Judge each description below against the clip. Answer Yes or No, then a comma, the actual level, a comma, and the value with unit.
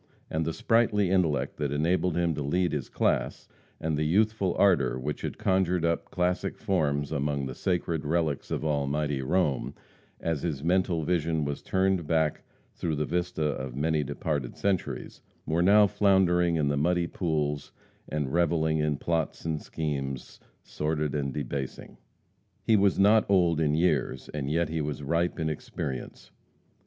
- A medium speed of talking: Yes, average, 160 wpm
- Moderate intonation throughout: Yes, average, 3.3 semitones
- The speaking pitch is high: No, very low, 80 Hz